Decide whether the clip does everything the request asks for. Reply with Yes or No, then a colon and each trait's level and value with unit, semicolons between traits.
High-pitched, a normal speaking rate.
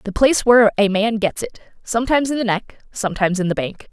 No: high, 215 Hz; fast, 215 wpm